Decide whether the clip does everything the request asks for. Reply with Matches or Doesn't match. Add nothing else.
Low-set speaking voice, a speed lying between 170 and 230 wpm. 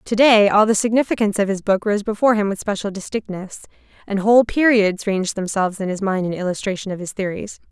Doesn't match